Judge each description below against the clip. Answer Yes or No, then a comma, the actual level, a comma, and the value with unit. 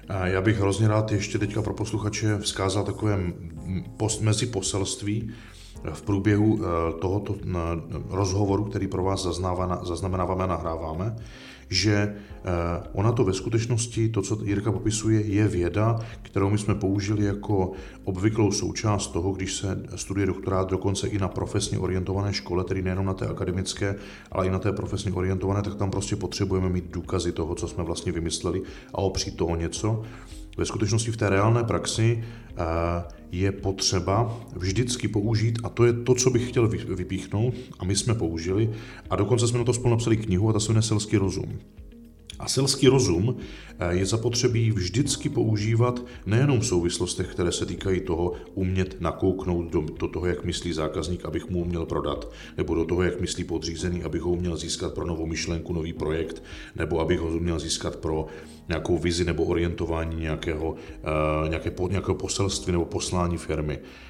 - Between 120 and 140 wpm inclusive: No, average, 160 wpm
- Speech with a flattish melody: No, average, 3.7 semitones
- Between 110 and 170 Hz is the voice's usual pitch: No, very low, 95 Hz